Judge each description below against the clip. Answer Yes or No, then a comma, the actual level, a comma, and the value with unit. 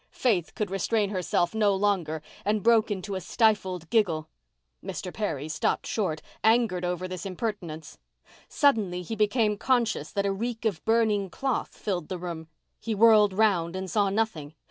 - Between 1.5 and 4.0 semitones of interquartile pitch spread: Yes, average, 3.7 semitones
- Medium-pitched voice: No, high, 200 Hz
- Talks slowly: No, average, 160 wpm